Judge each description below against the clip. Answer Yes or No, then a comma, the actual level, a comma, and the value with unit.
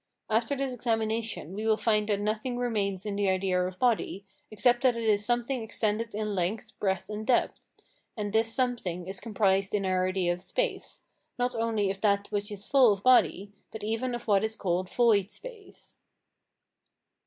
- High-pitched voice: Yes, high, 215 Hz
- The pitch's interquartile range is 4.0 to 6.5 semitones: No, average, 3.1 semitones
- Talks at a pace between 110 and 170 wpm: No, average, 180 wpm